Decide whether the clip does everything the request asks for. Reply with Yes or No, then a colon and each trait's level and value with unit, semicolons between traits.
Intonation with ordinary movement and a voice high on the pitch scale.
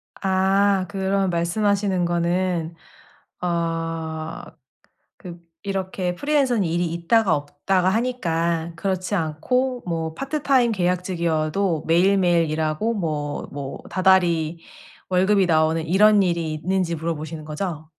No: average, 3.1 semitones; medium, 175 Hz